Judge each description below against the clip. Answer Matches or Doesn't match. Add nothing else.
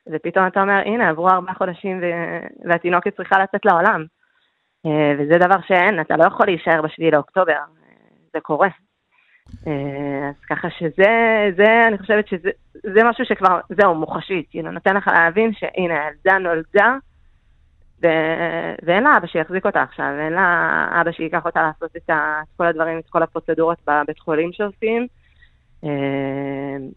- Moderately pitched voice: Matches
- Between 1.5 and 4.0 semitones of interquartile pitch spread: Matches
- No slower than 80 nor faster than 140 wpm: Doesn't match